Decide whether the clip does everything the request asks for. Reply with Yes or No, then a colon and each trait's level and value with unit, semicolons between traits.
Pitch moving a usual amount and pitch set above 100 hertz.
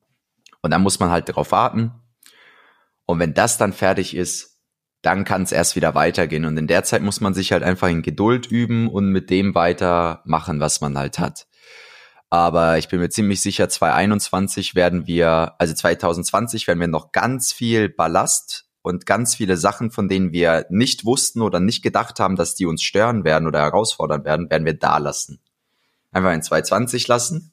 No: average, 3.7 semitones; very low, 95 Hz